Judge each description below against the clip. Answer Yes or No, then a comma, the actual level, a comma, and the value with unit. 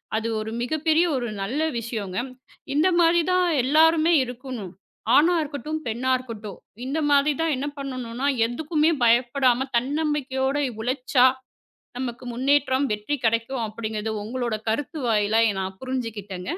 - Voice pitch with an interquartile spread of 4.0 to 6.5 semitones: Yes, average, 4.4 semitones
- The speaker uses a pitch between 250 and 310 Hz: Yes, very high, 255 Hz